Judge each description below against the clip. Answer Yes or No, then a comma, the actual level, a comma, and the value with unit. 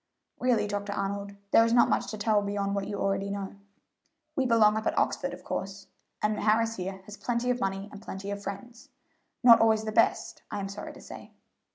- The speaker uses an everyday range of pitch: No, narrow, 2.2 semitones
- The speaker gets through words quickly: Yes, fast, 210 wpm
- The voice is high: Yes, high, 205 Hz